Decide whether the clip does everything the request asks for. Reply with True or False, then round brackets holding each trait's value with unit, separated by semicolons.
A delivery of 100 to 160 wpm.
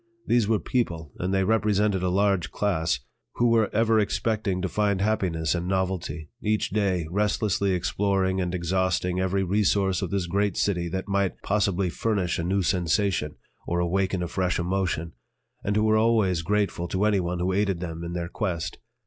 False (175 wpm)